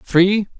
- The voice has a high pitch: Yes, high, 195 Hz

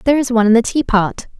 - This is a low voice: No, high, 235 Hz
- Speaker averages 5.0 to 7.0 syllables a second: No, 7.6 syllables/s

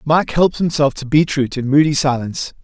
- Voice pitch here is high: No, medium, 145 Hz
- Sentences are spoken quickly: No, average, 180 wpm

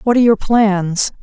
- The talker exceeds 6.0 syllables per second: No, 4.8 syllables/s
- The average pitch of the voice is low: No, high, 210 Hz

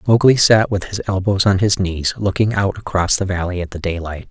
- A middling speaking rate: No, fast, 225 wpm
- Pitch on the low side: Yes, very low, 95 Hz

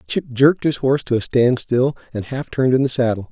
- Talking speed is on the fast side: Yes, fast, 255 wpm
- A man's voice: Yes, male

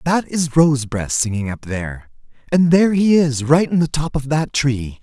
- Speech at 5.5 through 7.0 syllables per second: No, 4.9 syllables/s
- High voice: No, medium, 140 Hz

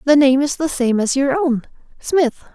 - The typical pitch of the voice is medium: No, very high, 280 Hz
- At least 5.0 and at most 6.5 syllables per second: No, 4.5 syllables/s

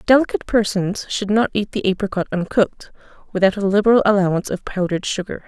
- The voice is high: Yes, high, 200 Hz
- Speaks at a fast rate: No, average, 165 wpm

